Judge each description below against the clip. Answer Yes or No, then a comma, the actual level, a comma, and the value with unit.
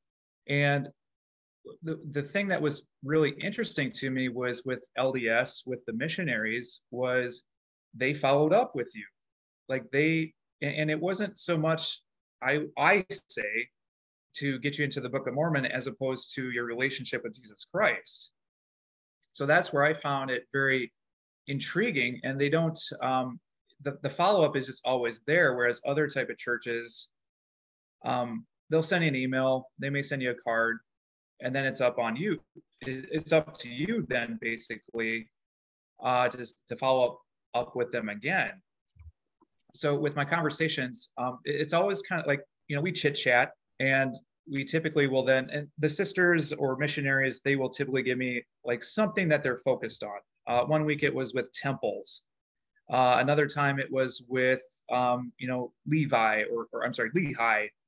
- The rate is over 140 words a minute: Yes, average, 170 wpm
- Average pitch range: Yes, average, 3.4 semitones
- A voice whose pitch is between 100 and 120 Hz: No, low, 135 Hz